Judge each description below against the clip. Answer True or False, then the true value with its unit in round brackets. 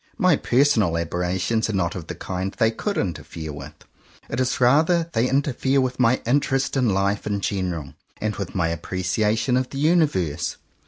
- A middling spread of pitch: False (6.5 semitones)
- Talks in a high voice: False (110 Hz)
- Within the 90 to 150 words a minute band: False (180 wpm)